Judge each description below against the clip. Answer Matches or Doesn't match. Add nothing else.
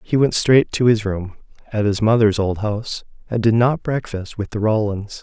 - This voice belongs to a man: Matches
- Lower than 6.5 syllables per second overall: Matches